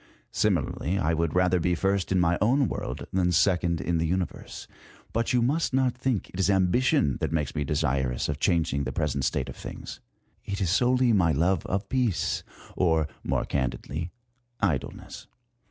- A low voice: Yes, very low, 90 Hz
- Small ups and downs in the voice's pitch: No, average, 4.1 semitones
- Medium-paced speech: Yes, average, 175 wpm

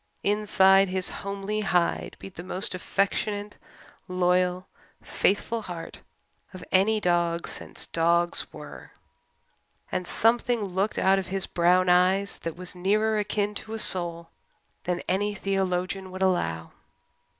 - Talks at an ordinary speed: No, slow, 130 wpm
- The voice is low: No, medium, 185 Hz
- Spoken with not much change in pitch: Yes, narrow, 2.2 semitones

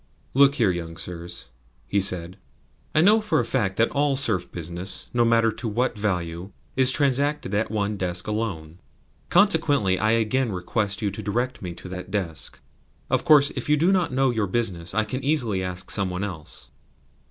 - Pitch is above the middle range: No, low, 105 Hz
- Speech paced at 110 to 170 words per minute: No, average, 185 wpm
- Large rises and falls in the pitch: Yes, wide, 6.1 semitones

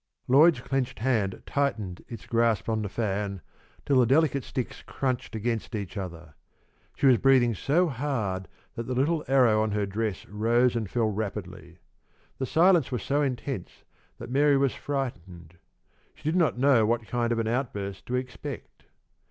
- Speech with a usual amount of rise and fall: Yes, average, 4.5 semitones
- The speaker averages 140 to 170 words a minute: Yes, average, 165 wpm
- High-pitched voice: No, low, 120 Hz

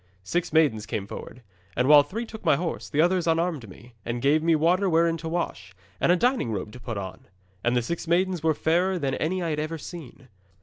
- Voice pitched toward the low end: No, medium, 160 Hz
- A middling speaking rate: No, fast, 225 wpm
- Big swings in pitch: Yes, wide, 5.7 semitones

